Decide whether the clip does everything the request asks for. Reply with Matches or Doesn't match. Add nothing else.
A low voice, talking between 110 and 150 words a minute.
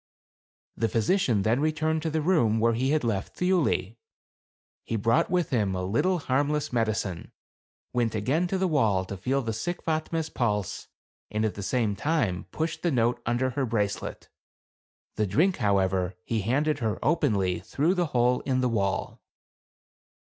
Doesn't match